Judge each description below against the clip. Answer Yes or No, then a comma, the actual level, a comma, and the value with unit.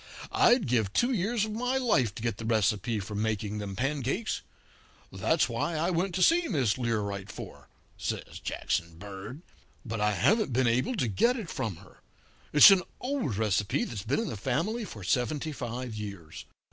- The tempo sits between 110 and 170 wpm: No, average, 180 wpm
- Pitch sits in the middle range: No, low, 120 Hz